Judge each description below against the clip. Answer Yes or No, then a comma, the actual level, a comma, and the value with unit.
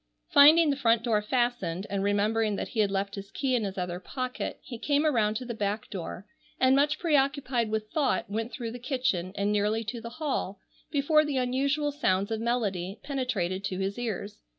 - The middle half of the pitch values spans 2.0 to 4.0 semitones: No, average, 4.8 semitones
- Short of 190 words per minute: No, average, 195 wpm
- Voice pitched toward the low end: No, high, 230 Hz